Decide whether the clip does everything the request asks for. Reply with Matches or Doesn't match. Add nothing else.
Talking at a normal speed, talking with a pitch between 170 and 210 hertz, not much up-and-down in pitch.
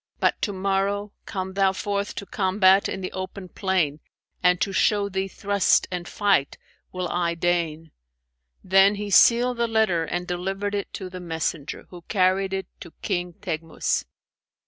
Matches